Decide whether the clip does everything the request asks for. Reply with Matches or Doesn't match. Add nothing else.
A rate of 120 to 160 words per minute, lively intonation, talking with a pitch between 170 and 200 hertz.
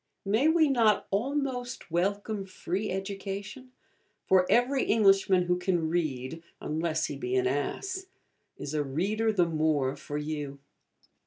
Matches